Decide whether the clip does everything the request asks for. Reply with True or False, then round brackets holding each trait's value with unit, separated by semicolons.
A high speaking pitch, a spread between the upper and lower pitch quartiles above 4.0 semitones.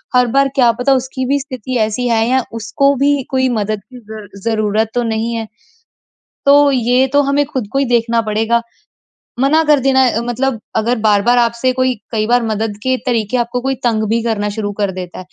False (240 Hz; 3.0 semitones)